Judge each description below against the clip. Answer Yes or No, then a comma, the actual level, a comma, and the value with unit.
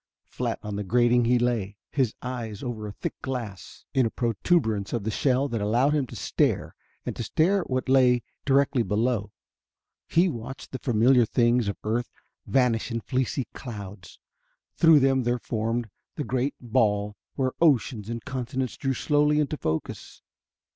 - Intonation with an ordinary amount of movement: Yes, average, 3.3 semitones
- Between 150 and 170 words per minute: Yes, average, 160 wpm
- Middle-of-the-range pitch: No, low, 120 Hz